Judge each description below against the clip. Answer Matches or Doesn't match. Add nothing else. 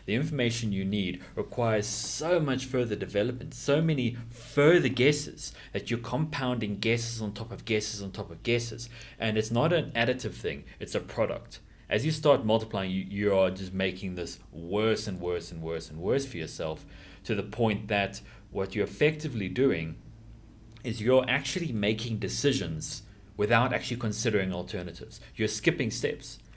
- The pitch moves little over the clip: Doesn't match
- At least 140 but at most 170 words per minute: Matches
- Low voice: Matches